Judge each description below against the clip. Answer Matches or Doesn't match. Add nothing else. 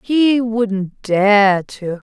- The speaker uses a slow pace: Matches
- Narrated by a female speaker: Matches